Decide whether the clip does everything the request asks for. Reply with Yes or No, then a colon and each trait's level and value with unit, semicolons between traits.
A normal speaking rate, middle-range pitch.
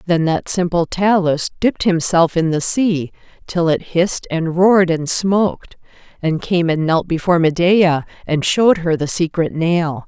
Yes: average, 165 wpm; medium, 170 Hz